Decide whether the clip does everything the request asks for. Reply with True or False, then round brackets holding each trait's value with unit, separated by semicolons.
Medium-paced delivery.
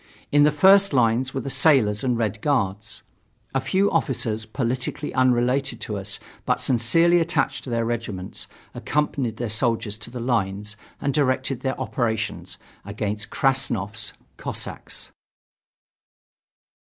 False (130 wpm)